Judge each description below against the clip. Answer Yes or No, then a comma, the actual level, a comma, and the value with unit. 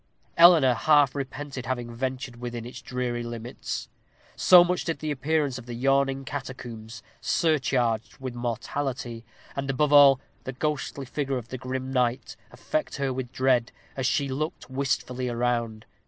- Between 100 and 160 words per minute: Yes, average, 150 wpm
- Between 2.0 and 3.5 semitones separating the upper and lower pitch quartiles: Yes, narrow, 2.5 semitones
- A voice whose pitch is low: Yes, low, 130 Hz